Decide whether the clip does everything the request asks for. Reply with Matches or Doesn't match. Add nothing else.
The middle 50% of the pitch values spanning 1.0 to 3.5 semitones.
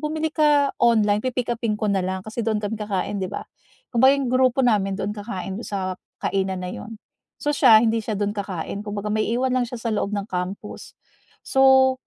Doesn't match